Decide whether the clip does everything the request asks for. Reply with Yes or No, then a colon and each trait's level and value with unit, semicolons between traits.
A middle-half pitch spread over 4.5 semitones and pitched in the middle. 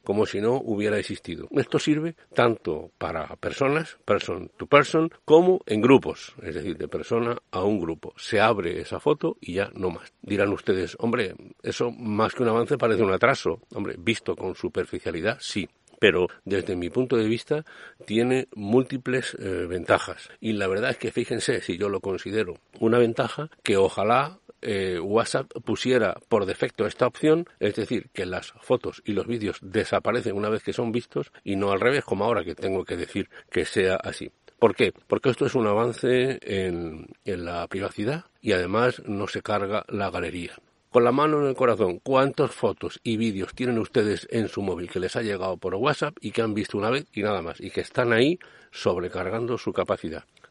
No: average, 4.9 semitones; low, 115 Hz